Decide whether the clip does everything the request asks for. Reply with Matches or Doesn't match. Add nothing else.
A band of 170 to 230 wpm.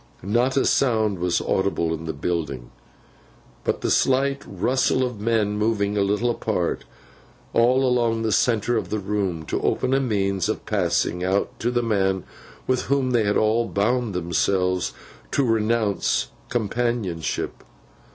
Doesn't match